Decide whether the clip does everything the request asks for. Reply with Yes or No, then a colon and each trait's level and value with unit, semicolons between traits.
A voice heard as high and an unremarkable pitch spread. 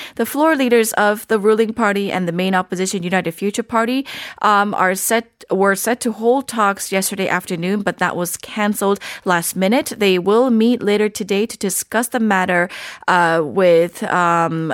Yes: high, 200 Hz; average, 3.6 semitones